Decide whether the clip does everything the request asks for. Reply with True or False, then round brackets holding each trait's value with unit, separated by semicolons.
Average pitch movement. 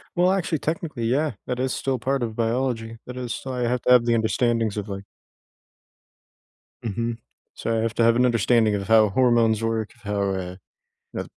False (2.1 semitones)